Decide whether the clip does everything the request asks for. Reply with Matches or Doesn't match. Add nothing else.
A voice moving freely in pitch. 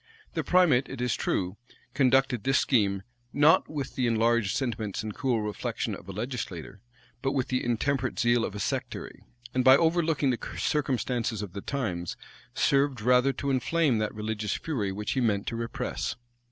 Doesn't match